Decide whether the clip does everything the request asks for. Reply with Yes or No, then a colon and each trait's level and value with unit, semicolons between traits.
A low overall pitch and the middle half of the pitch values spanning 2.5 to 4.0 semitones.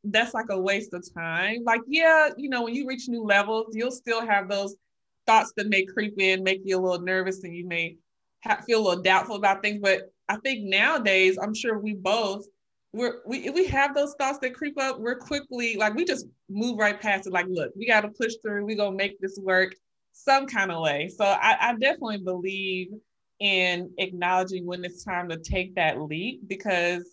No: high, 200 Hz; average, 3.7 semitones